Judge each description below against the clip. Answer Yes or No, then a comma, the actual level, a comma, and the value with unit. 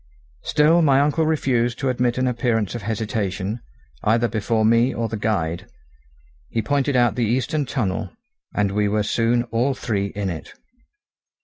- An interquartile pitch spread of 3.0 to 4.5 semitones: Yes, average, 3.5 semitones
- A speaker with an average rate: Yes, average, 155 wpm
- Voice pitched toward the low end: Yes, low, 115 Hz